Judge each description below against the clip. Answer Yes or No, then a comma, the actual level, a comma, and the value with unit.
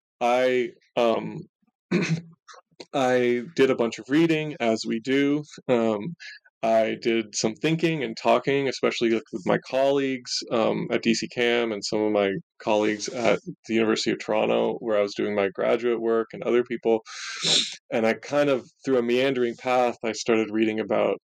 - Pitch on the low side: Yes, low, 120 Hz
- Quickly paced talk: No, average, 165 wpm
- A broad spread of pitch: No, average, 3.7 semitones